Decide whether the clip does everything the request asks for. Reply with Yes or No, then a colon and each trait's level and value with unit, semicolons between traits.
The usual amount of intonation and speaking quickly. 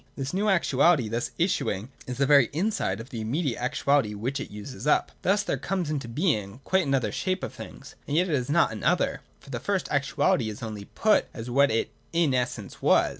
No: wide, 6.5 semitones; fast, 220 wpm